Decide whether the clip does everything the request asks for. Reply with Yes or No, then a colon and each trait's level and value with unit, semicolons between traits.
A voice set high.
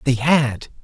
No: low, 135 Hz